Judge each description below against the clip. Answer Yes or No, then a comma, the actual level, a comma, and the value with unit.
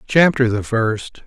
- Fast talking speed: No, average, 140 wpm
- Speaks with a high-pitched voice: No, low, 120 Hz